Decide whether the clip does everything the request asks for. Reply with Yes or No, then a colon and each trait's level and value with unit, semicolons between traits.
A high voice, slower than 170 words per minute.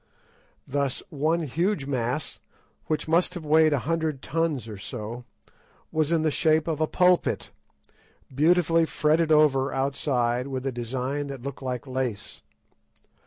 No: medium, 145 Hz; average, 140 wpm